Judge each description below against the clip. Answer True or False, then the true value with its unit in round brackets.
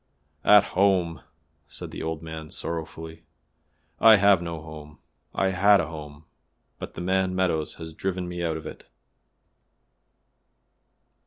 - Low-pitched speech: True (85 Hz)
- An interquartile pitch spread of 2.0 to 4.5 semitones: True (2.9 semitones)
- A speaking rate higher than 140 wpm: False (135 wpm)